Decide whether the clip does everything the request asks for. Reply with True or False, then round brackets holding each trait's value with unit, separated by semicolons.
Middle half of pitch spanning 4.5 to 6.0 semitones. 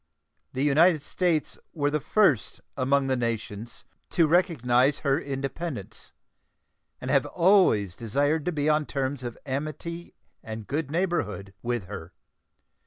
True (4.9 semitones)